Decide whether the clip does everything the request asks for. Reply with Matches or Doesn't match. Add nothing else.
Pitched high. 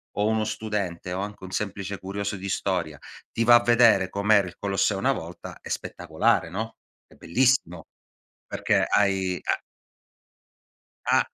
Doesn't match